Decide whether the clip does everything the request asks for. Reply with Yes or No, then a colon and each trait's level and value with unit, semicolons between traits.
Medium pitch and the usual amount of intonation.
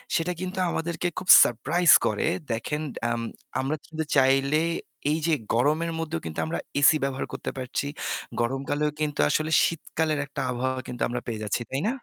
Yes: medium, 145 Hz; average, 3.7 semitones